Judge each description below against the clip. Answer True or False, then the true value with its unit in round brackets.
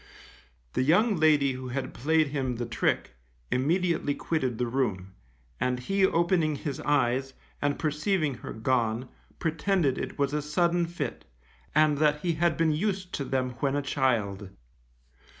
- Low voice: False (145 Hz)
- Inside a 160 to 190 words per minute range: False (150 wpm)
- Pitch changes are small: False (4.1 semitones)